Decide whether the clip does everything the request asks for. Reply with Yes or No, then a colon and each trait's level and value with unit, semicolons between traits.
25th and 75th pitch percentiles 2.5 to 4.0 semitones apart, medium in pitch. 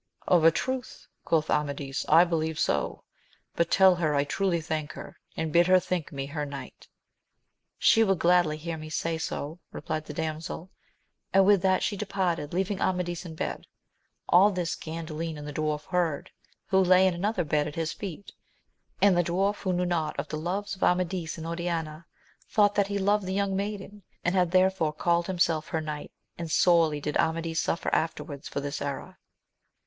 Yes: average, 3.2 semitones; medium, 170 Hz